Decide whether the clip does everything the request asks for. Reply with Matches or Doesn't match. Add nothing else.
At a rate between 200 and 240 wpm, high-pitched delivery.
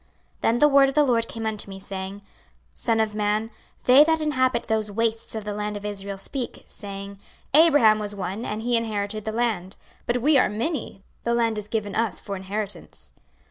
Matches